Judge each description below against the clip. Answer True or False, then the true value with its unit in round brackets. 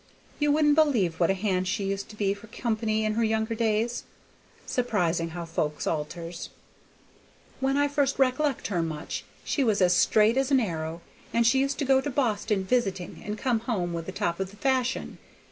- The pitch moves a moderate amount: False (5.9 semitones)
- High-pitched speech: True (215 Hz)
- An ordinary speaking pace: True (195 wpm)